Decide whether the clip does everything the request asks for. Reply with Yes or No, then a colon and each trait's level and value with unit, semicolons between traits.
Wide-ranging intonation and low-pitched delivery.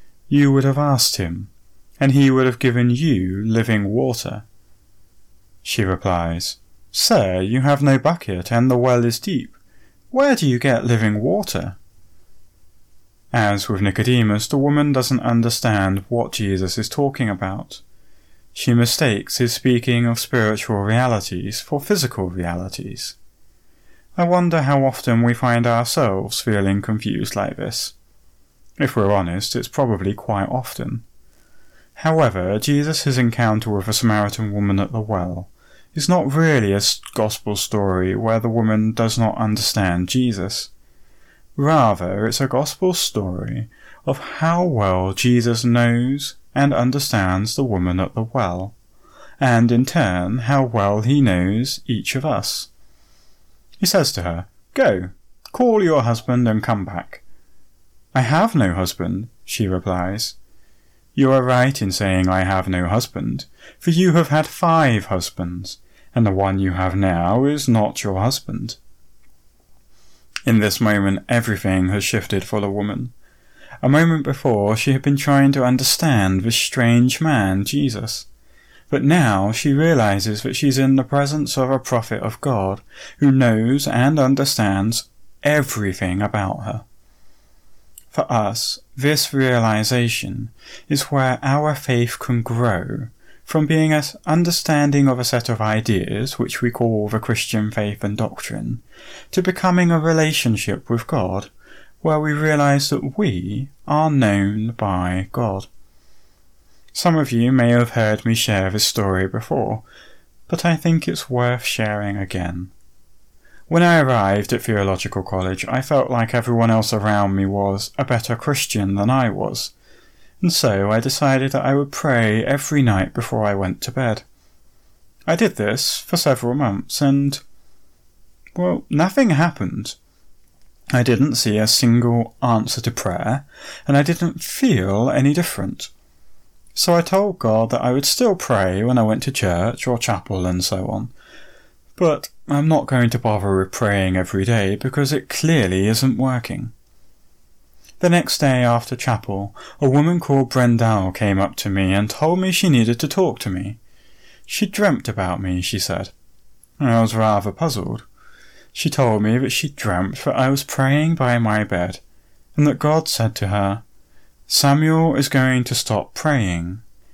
Yes: wide, 5.7 semitones; low, 115 Hz